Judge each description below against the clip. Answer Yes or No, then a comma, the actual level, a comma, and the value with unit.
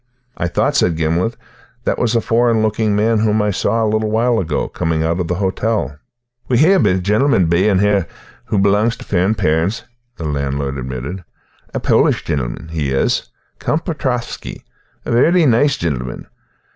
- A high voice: No, low, 100 Hz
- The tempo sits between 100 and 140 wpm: No, average, 170 wpm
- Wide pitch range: Yes, wide, 5.7 semitones